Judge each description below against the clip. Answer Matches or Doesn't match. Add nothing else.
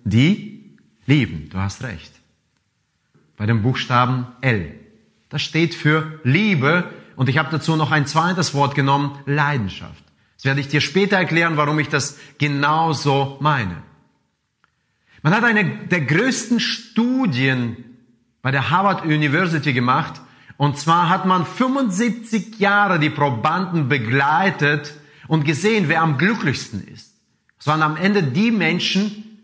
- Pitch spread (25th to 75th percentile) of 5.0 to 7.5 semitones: Matches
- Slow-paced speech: Doesn't match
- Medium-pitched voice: Matches